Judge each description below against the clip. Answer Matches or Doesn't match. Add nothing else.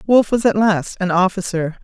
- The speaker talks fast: Doesn't match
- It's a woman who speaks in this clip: Matches